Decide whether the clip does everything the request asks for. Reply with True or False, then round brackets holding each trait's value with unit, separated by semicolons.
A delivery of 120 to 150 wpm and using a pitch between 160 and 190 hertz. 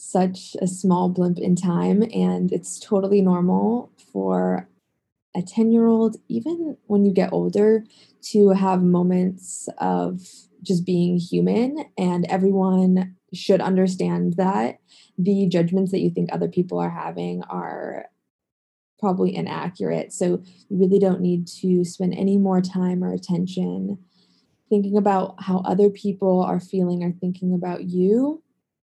True (140 wpm; 185 Hz)